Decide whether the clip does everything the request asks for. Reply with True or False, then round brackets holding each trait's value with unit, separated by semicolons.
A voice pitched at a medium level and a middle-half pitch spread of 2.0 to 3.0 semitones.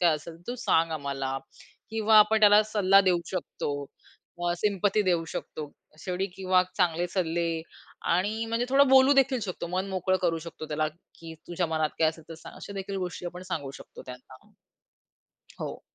False (180 Hz; 4.0 semitones)